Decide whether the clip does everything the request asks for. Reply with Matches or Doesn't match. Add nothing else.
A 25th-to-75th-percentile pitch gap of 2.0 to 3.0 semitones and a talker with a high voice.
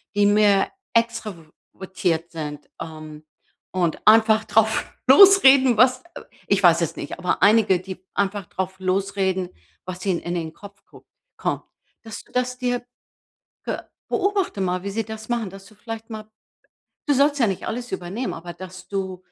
Doesn't match